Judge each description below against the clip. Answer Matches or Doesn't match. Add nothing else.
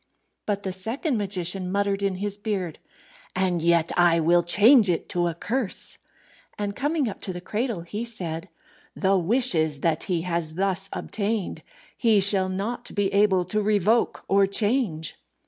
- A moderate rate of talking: Matches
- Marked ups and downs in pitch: Doesn't match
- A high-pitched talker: Matches